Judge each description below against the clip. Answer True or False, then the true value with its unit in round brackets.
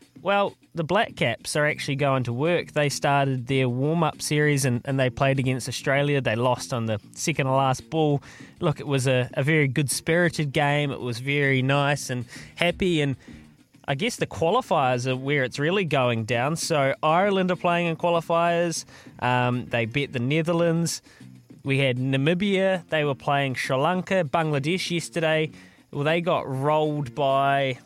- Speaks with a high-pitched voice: False (140 Hz)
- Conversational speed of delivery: True (170 wpm)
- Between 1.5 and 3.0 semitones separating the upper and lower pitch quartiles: False (3.7 semitones)